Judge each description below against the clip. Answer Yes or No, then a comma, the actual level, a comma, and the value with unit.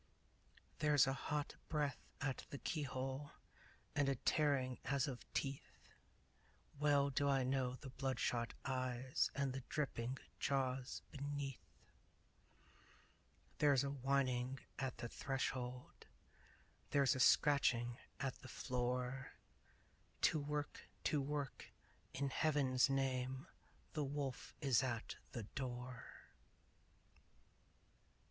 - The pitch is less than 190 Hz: Yes, low, 135 Hz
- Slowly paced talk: Yes, slow, 105 wpm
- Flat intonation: Yes, narrow, 1.8 semitones